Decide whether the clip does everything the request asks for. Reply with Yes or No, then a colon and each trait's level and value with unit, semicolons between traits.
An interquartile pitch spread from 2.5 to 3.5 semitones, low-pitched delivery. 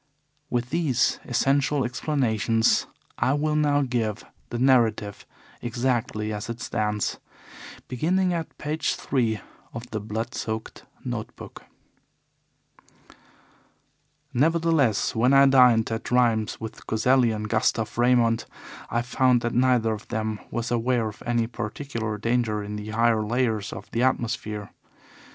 Yes: average, 2.8 semitones; low, 120 Hz